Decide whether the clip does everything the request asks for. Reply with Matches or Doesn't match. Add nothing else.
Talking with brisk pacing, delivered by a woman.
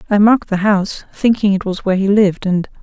Matches